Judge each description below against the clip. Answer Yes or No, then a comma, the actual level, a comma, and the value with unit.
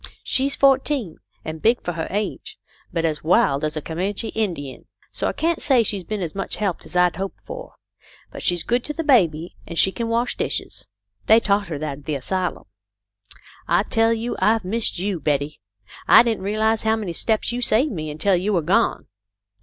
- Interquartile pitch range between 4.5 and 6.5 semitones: Yes, wide, 5.5 semitones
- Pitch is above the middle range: Yes, high, 200 Hz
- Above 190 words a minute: Yes, average, 200 wpm